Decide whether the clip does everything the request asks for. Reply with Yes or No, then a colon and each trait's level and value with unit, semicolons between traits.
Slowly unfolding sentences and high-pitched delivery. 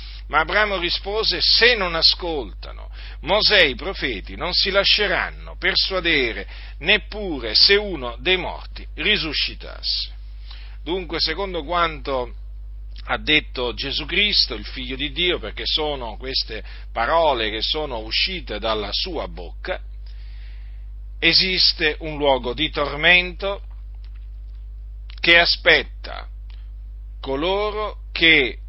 No: slow, 105 wpm; low, 135 Hz